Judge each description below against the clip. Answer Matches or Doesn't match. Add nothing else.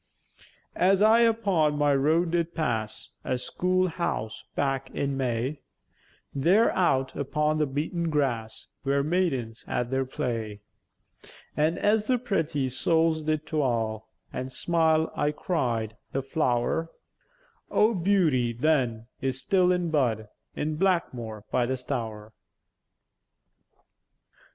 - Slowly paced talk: Matches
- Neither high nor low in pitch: Matches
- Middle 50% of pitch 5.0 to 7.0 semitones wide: Matches